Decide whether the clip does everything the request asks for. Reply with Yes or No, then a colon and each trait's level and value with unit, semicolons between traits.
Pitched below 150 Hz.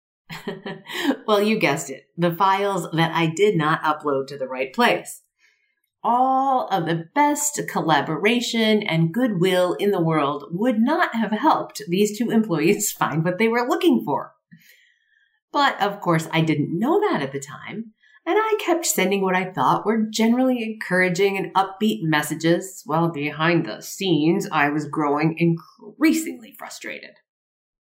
No: high, 195 Hz